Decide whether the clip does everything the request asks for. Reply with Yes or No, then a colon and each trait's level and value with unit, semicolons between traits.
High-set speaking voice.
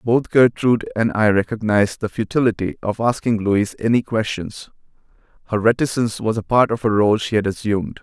No: low, 110 Hz